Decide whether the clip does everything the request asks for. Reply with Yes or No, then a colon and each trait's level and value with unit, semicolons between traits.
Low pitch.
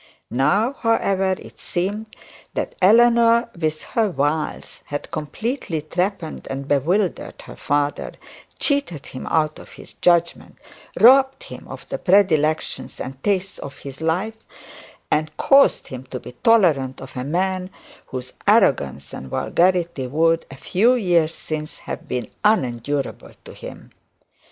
No: medium, 170 Hz